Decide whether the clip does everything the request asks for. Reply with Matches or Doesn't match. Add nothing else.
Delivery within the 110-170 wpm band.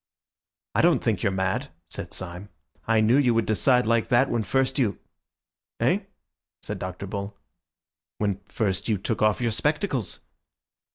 Matches